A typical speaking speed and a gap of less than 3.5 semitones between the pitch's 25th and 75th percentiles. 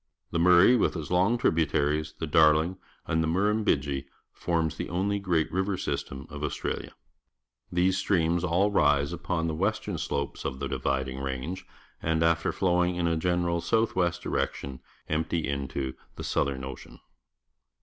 No: average, 155 wpm; average, 3.9 semitones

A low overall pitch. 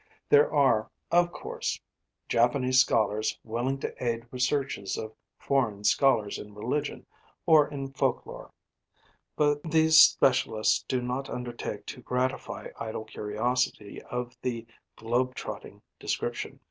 Yes: low, 125 Hz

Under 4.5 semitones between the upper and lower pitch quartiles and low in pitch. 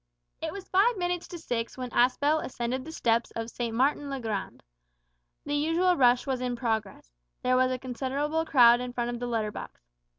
No: average, 3.7 semitones; very high, 255 Hz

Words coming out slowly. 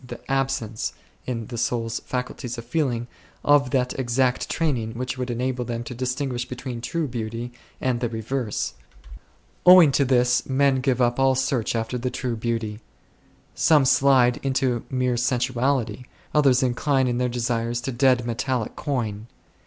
No: average, 155 wpm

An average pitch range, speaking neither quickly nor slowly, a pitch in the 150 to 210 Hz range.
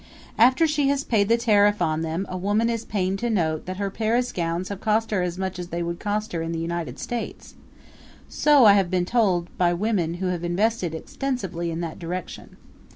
No: average, 4.4 semitones; fast, 215 wpm; high, 190 Hz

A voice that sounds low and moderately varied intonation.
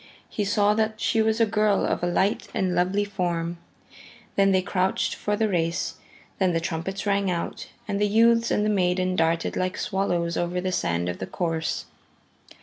No: high, 190 Hz; average, 3.0 semitones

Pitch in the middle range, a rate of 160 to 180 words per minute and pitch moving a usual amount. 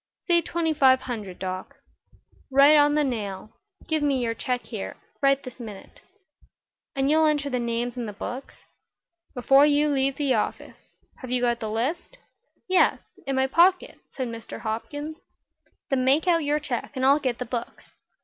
No: very high, 265 Hz; average, 170 wpm; average, 3.6 semitones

